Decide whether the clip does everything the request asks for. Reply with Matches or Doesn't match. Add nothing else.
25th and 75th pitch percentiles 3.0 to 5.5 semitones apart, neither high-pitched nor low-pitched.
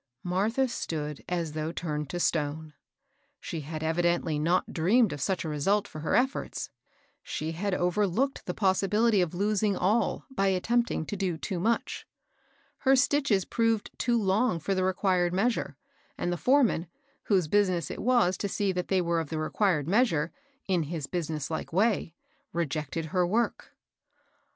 Matches